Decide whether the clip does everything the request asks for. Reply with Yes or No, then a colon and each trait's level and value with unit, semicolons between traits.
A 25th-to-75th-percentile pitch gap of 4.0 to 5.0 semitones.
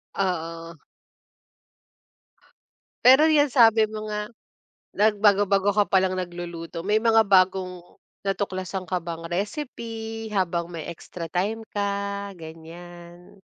No: average, 3.5 semitones